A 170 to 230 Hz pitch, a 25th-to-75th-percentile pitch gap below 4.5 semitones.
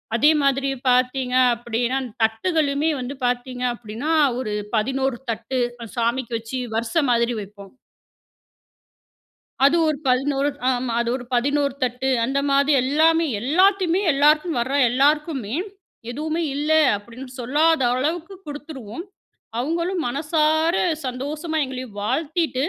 No: very high, 270 Hz; average, 4.0 semitones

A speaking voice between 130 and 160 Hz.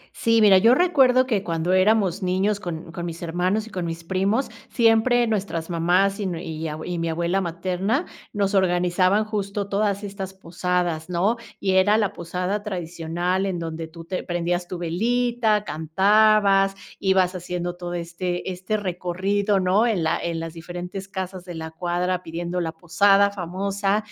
No: medium, 185 Hz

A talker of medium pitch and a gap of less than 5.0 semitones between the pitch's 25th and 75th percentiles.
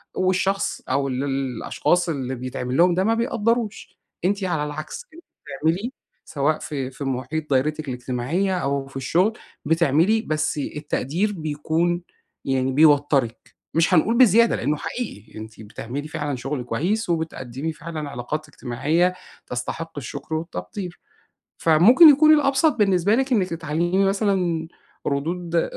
No: medium, 160 Hz; wide, 5.5 semitones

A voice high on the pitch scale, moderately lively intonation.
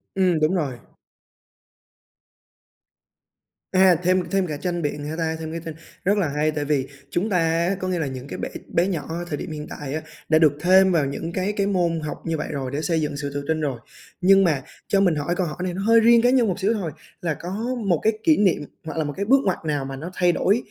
No: medium, 170 Hz; average, 4.0 semitones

